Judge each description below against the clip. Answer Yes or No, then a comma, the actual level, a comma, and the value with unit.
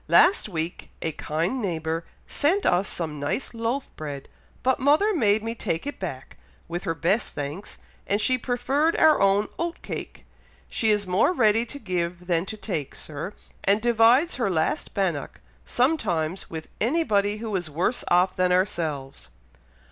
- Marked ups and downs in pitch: Yes, wide, 6.4 semitones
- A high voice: Yes, high, 200 Hz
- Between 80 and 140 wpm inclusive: No, average, 160 wpm